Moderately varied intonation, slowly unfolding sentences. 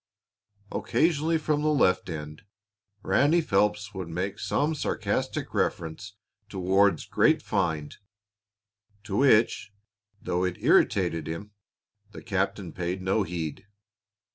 Yes: average, 4.3 semitones; slow, 110 wpm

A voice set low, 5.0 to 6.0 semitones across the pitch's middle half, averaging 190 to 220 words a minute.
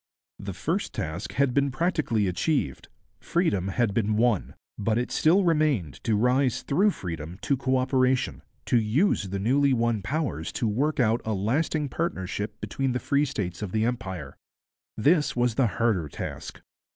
No: low, 120 Hz; average, 5.3 semitones; average, 165 wpm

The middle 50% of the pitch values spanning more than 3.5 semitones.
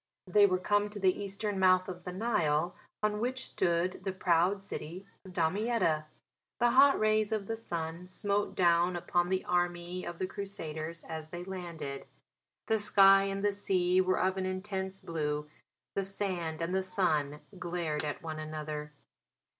No: average, 3.0 semitones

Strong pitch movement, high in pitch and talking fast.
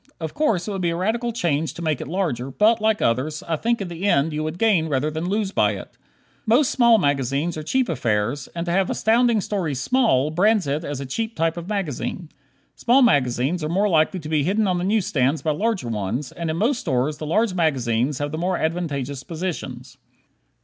No: wide, 6.1 semitones; medium, 165 Hz; fast, 215 wpm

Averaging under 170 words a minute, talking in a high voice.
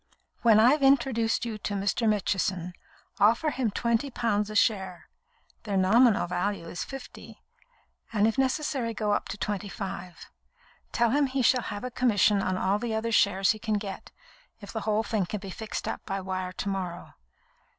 No: average, 180 wpm; high, 210 Hz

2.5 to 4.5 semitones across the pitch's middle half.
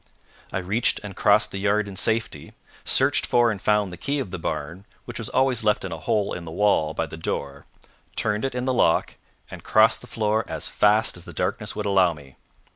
Yes: average, 4.0 semitones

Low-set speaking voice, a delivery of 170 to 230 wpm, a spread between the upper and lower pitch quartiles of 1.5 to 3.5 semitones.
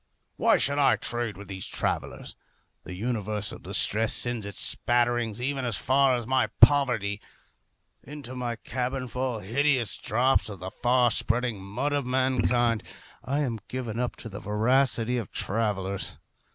No: low, 120 Hz; average, 150 wpm; average, 3.2 semitones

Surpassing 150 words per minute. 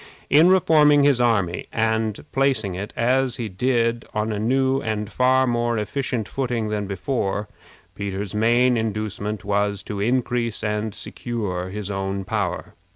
No: average, 145 wpm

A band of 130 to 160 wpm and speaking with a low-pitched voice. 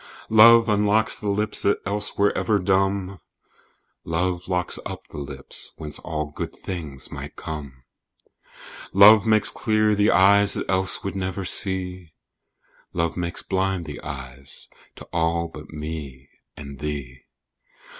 Yes: slow, 135 wpm; very low, 90 Hz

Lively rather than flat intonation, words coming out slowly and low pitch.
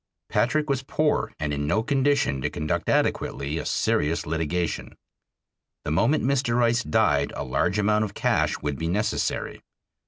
No: wide, 8.4 semitones; average, 155 wpm; low, 105 Hz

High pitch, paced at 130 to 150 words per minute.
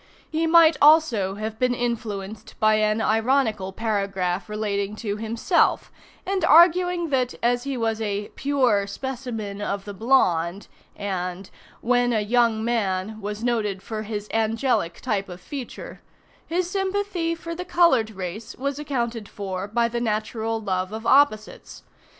Yes: high, 225 Hz; average, 145 wpm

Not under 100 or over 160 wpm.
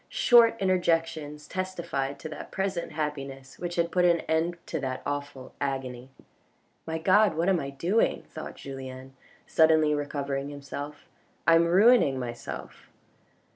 Yes: average, 150 wpm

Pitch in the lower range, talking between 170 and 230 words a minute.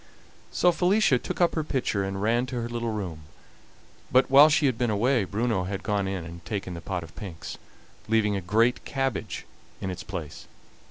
Yes: low, 105 Hz; average, 195 wpm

